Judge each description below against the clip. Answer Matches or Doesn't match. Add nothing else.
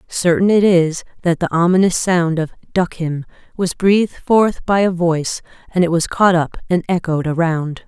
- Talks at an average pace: Matches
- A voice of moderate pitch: Matches